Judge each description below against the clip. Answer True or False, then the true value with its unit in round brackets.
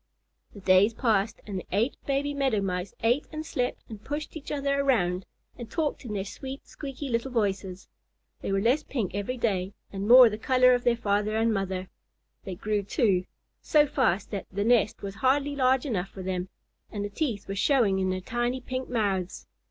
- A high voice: True (220 Hz)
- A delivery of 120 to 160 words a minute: False (195 wpm)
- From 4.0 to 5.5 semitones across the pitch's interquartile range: True (4.8 semitones)